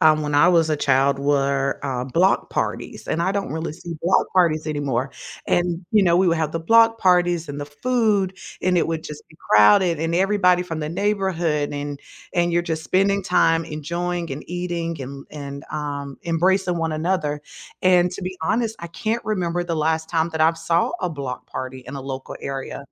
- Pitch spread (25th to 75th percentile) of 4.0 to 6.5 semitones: No, average, 3.6 semitones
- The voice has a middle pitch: Yes, medium, 165 Hz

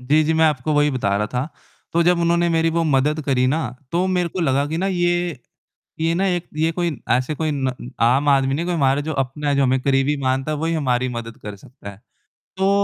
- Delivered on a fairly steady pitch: No, average, 4.1 semitones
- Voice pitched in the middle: Yes, medium, 150 Hz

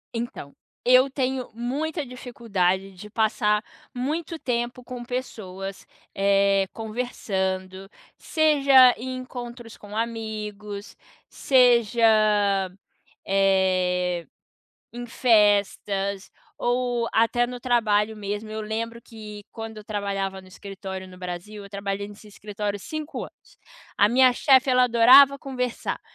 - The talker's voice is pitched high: Yes, high, 220 Hz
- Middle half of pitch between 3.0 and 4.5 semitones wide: Yes, average, 3.9 semitones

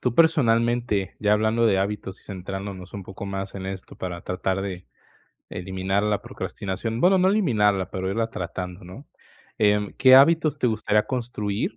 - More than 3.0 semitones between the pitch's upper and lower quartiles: Yes, average, 3.5 semitones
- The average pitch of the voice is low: Yes, low, 105 Hz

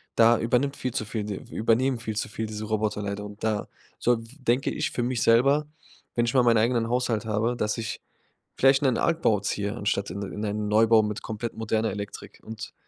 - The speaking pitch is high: No, low, 110 Hz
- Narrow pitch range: Yes, narrow, 2.3 semitones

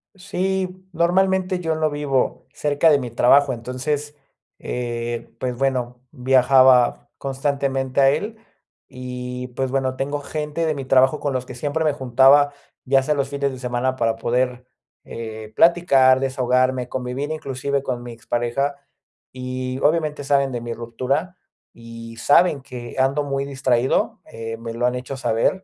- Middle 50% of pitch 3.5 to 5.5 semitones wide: No, narrow, 2.5 semitones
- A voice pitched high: No, low, 130 Hz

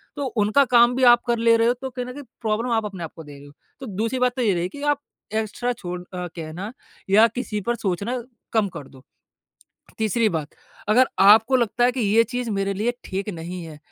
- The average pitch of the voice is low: No, high, 220 Hz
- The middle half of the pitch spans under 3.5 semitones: No, average, 4.5 semitones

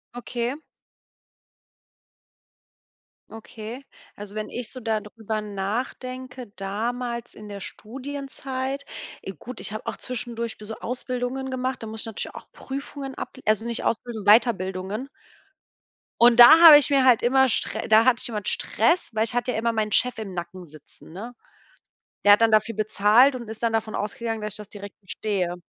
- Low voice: No, high, 230 Hz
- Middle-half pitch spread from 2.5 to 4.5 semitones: Yes, average, 3.0 semitones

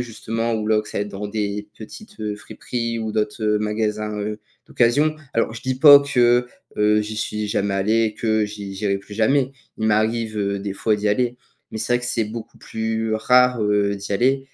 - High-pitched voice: No, low, 110 Hz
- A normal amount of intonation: No, narrow, 2.0 semitones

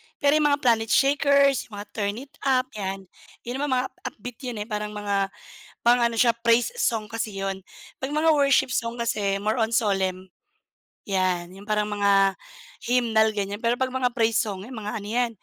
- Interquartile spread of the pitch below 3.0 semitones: No, average, 3.6 semitones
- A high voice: Yes, high, 225 Hz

